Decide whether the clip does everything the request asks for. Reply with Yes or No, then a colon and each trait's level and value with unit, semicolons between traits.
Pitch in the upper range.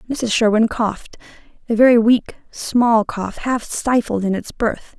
Yes: high, 225 Hz